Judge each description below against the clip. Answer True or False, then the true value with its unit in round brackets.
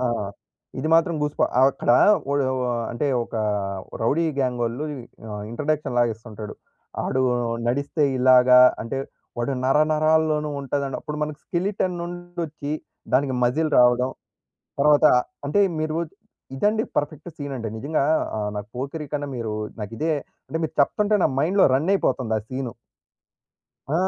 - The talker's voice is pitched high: False (145 Hz)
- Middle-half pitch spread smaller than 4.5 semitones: True (3.8 semitones)